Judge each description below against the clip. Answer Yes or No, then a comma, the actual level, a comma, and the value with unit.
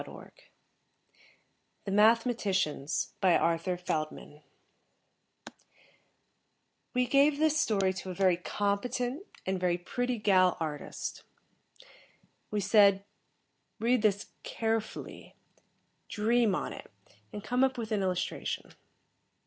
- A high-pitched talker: Yes, high, 205 Hz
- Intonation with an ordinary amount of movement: Yes, average, 4.6 semitones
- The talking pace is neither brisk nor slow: No, slow, 100 wpm